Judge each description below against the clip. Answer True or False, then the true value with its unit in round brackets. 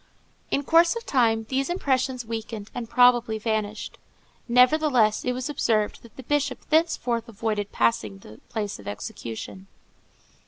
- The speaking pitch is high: True (235 Hz)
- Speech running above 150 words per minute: False (135 wpm)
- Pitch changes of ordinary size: True (3.6 semitones)